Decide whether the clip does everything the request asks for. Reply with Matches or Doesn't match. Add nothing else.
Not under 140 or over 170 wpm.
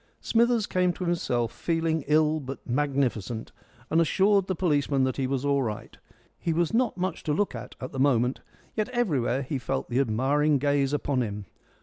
Doesn't match